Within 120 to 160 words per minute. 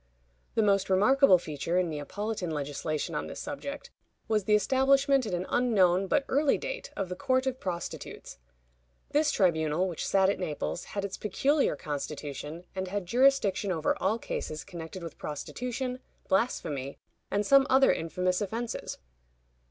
Yes: average, 150 wpm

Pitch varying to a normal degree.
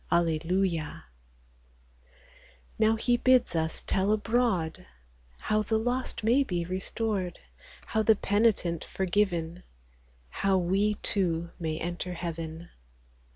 Yes: average, 4.3 semitones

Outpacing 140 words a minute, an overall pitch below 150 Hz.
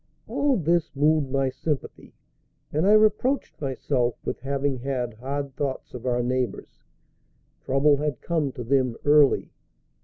No: slow, 135 wpm; medium, 140 Hz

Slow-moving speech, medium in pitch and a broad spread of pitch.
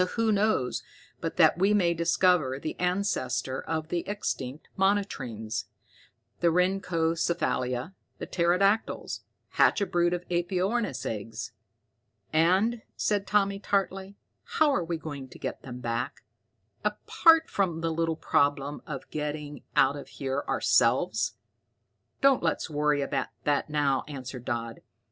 Yes: slow, 130 wpm; medium, 165 Hz; wide, 6.1 semitones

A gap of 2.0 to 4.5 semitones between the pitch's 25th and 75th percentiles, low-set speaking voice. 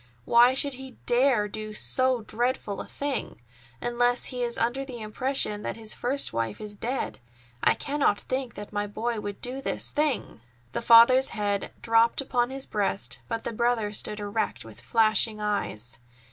No: average, 3.6 semitones; high, 230 Hz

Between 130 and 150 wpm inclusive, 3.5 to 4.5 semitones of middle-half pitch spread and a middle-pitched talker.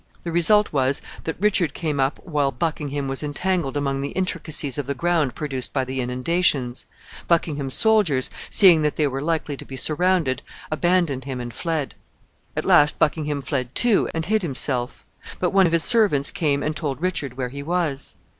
No: average, 180 wpm; average, 4.0 semitones; medium, 150 Hz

